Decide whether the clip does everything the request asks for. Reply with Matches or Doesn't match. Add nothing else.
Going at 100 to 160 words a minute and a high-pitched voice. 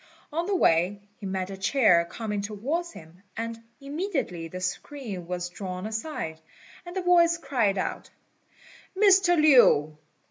Matches